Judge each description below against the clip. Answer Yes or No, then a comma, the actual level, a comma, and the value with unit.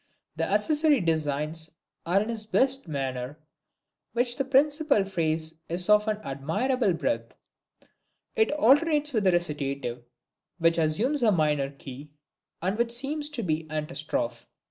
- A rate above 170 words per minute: No, average, 140 wpm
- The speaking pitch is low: No, medium, 180 Hz